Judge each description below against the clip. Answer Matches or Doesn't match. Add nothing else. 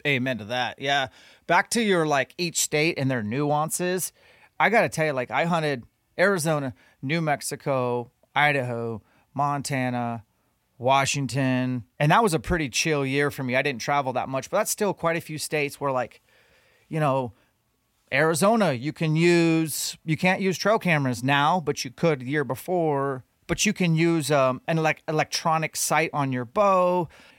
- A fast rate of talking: Doesn't match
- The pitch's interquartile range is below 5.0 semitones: Matches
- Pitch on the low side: Doesn't match